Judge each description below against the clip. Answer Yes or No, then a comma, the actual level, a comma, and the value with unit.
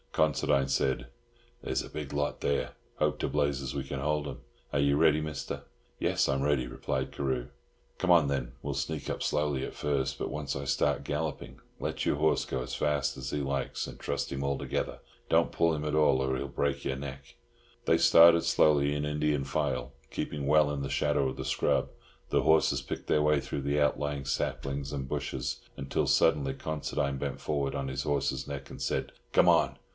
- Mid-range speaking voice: No, very low, 70 Hz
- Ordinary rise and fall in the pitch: No, narrow, 1.6 semitones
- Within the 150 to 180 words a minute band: No, average, 195 wpm